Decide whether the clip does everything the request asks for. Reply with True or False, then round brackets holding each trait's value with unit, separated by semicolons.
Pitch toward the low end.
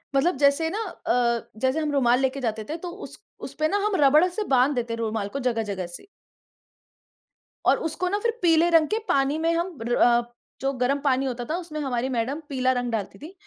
False (275 Hz)